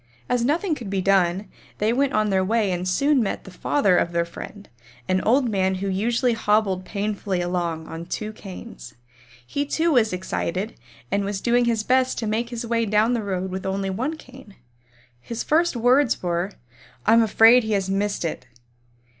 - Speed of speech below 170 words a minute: No, average, 185 wpm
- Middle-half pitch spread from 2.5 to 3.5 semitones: No, average, 4.0 semitones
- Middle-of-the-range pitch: No, high, 210 Hz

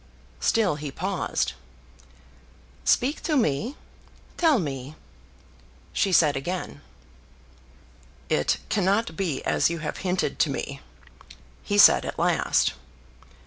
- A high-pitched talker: No, medium, 180 Hz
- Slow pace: Yes, slow, 105 wpm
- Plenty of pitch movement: Yes, wide, 5.8 semitones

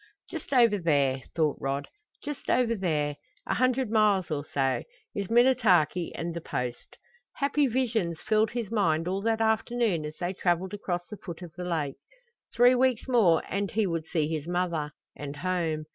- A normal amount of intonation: No, wide, 6.0 semitones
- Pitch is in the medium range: Yes, medium, 180 Hz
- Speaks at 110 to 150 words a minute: No, average, 175 wpm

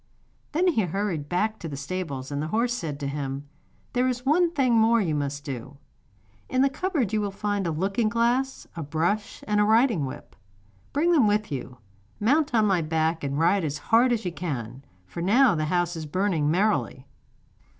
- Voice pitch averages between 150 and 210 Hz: Yes, high, 190 Hz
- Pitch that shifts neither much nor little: No, wide, 7.5 semitones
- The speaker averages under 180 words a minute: No, average, 195 wpm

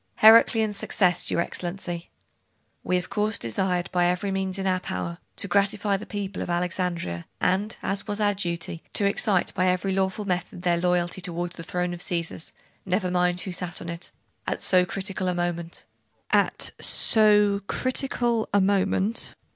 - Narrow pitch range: Yes, narrow, 2.3 semitones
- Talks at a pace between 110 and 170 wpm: Yes, average, 165 wpm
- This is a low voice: No, medium, 185 Hz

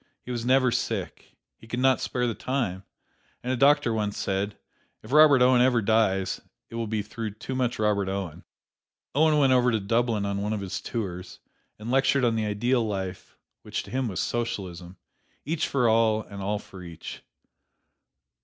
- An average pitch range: Yes, average, 4.0 semitones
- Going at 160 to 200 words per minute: Yes, average, 180 wpm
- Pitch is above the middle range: No, low, 115 Hz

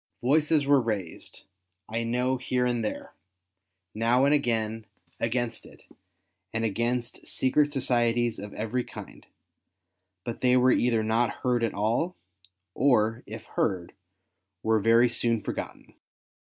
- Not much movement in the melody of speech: Yes, narrow, 2.1 semitones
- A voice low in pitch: Yes, low, 120 Hz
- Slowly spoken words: Yes, slow, 125 wpm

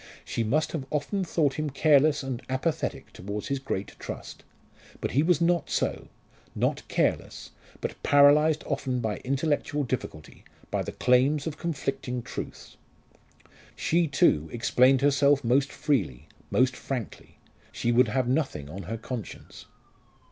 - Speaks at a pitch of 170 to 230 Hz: No, low, 135 Hz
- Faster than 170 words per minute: No, average, 140 wpm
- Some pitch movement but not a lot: Yes, average, 3.4 semitones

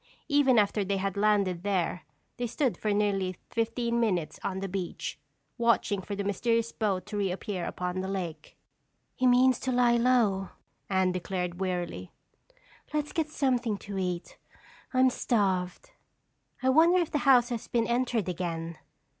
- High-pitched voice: Yes, high, 205 Hz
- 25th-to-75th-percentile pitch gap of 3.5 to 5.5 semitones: Yes, average, 4.7 semitones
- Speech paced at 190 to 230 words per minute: No, average, 155 wpm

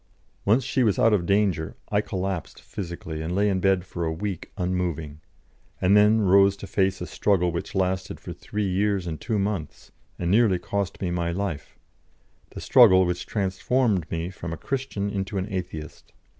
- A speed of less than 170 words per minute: No, average, 180 wpm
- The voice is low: Yes, very low, 95 Hz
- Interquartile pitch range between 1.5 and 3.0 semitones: Yes, average, 2.7 semitones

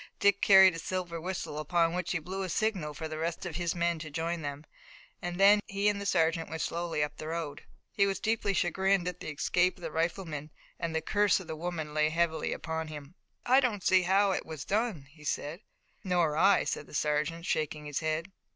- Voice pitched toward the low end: No, medium, 170 Hz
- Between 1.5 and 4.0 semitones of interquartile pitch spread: Yes, average, 3.4 semitones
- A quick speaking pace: Yes, fast, 220 wpm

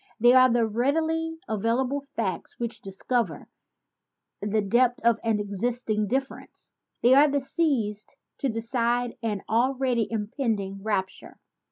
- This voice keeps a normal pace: No, slow, 120 wpm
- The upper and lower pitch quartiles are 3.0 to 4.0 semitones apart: Yes, average, 3.4 semitones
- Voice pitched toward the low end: No, high, 235 Hz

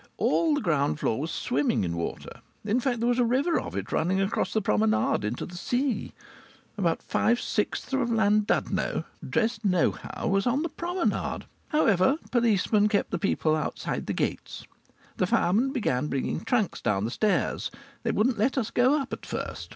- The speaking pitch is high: Yes, high, 210 Hz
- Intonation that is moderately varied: No, wide, 7.1 semitones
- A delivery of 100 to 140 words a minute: No, average, 175 wpm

